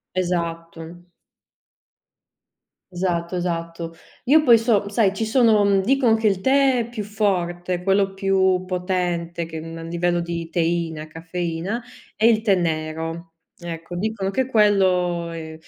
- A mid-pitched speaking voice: Yes, medium, 180 Hz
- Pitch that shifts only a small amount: No, average, 3.5 semitones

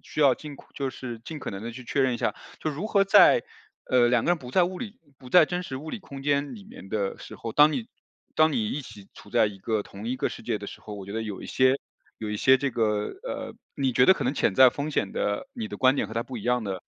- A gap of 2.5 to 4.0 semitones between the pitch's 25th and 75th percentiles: No, wide, 5.4 semitones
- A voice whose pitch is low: Yes, low, 130 Hz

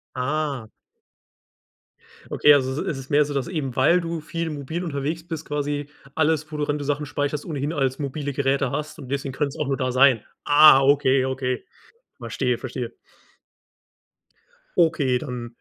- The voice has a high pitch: No, medium, 145 Hz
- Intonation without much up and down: Yes, narrow, 2.2 semitones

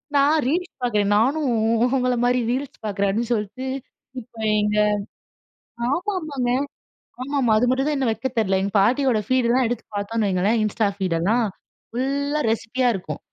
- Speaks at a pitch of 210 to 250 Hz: Yes, high, 245 Hz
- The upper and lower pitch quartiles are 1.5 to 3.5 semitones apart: No, average, 4.3 semitones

